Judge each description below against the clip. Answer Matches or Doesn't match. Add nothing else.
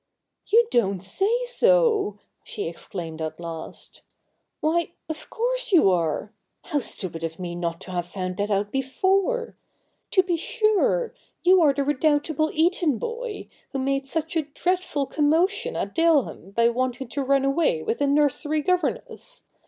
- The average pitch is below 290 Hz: Doesn't match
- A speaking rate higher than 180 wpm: Doesn't match